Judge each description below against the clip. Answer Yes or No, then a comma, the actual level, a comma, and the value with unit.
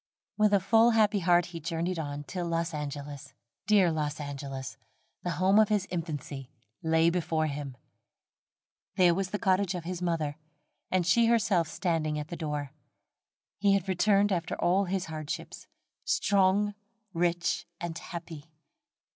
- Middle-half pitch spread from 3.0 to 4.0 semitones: Yes, average, 3.6 semitones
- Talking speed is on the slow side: No, average, 145 wpm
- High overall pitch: No, medium, 170 Hz